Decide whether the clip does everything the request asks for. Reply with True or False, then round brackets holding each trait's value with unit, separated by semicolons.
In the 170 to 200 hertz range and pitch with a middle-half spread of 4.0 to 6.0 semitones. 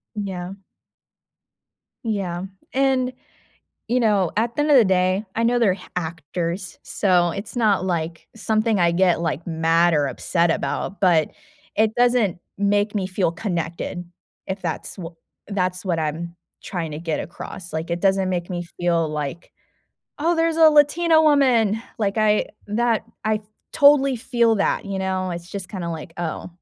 True (190 Hz; 4.6 semitones)